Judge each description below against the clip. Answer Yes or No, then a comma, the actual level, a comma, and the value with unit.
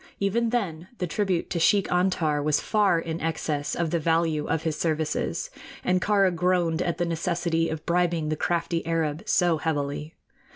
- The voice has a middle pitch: Yes, medium, 165 Hz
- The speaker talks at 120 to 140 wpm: No, average, 170 wpm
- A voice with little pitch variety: Yes, narrow, 2.2 semitones